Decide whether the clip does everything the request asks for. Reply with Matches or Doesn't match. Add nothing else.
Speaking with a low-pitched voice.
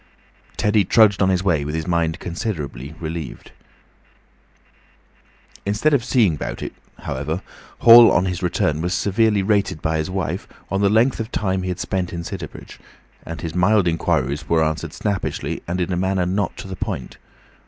Matches